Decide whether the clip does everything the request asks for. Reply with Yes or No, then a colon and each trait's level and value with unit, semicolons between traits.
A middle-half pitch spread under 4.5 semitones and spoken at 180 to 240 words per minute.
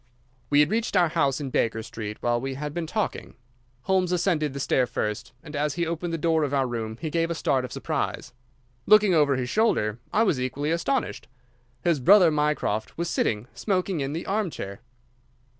No: average, 5.0 semitones; average, 190 wpm